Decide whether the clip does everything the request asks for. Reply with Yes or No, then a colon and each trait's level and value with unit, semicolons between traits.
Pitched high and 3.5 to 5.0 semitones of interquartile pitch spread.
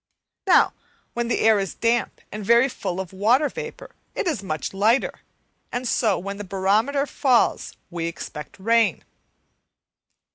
Yes: high, 220 Hz; average, 4.2 semitones